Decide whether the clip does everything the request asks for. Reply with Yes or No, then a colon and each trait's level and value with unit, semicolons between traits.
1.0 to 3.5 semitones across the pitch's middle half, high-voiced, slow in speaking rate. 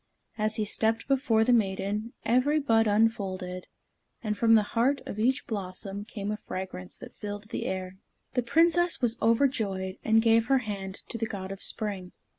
No: average, 2.9 semitones; high, 215 Hz; average, 175 wpm